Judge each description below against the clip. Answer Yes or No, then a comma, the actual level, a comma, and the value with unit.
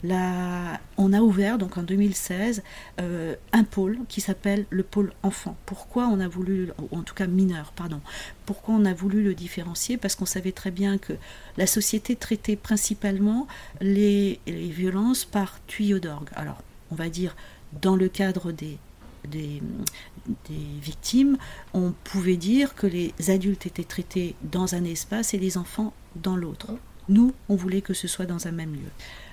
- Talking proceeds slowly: No, average, 170 wpm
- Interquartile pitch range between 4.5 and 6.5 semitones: No, average, 2.7 semitones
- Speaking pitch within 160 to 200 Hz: Yes, high, 190 Hz